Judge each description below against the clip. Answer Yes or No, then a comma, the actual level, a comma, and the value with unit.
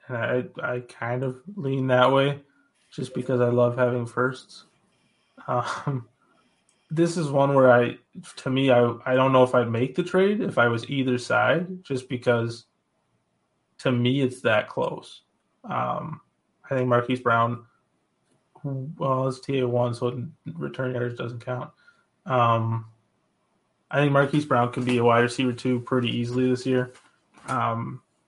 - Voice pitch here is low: Yes, low, 125 Hz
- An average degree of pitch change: No, narrow, 2.0 semitones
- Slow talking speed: No, average, 155 wpm